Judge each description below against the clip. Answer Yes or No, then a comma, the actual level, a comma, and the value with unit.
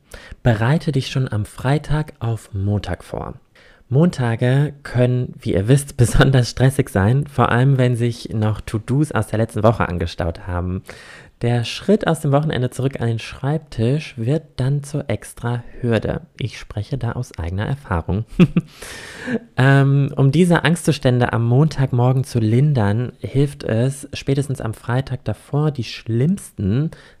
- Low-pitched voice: Yes, low, 125 Hz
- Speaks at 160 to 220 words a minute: No, average, 140 wpm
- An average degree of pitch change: Yes, average, 4.0 semitones